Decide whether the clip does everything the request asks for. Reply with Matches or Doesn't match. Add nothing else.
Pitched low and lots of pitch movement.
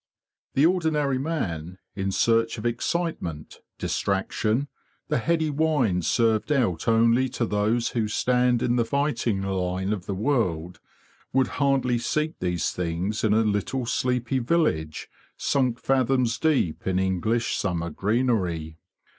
Matches